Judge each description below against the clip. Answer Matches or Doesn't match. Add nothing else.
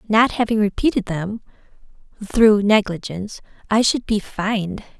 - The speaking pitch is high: Matches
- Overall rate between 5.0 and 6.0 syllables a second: Doesn't match